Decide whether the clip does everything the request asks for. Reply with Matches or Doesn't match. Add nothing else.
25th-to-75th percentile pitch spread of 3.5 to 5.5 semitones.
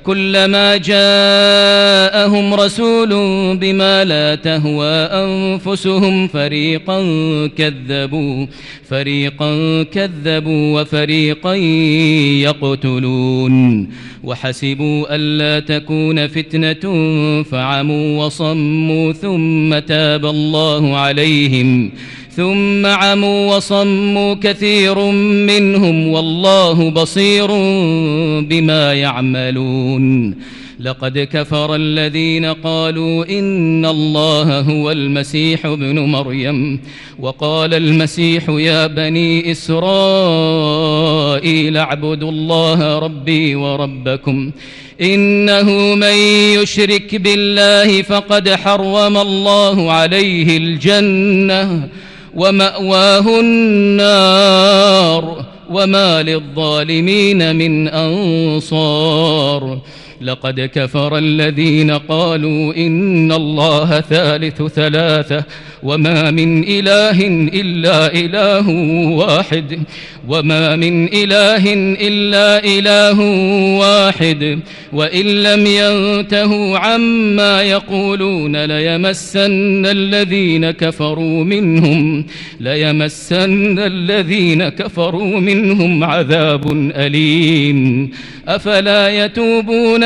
Matches